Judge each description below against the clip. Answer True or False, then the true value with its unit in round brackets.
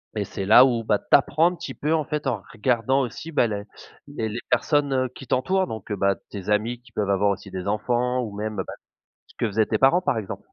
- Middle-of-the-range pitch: False (115 Hz)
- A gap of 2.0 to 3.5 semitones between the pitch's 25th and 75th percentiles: False (4.3 semitones)